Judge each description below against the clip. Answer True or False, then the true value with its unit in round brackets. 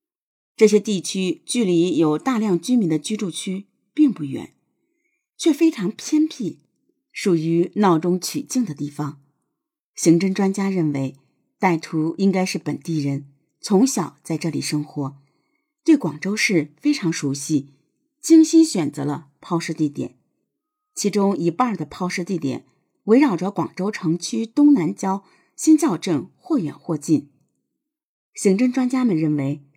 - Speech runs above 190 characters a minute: True (210 characters per minute)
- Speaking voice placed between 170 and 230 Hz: True (190 Hz)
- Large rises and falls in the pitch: True (8.8 semitones)